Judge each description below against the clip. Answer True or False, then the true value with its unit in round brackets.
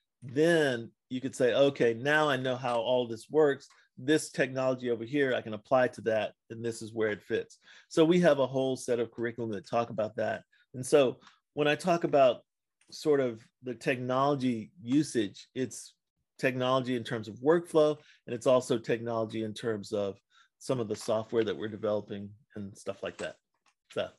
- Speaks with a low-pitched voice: True (125 Hz)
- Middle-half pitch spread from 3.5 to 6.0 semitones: True (3.9 semitones)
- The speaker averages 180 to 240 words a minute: True (185 wpm)